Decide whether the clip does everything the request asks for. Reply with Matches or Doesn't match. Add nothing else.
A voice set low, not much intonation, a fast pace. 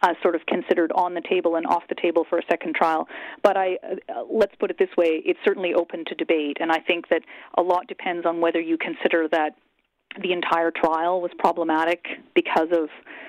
Doesn't match